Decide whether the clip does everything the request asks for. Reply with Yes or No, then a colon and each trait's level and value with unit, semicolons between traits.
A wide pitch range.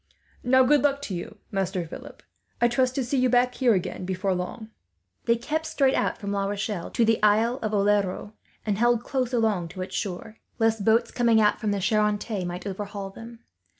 No: average, 3.4 semitones